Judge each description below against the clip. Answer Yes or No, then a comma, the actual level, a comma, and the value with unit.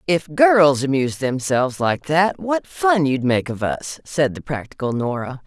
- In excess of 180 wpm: No, average, 175 wpm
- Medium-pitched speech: Yes, medium, 145 Hz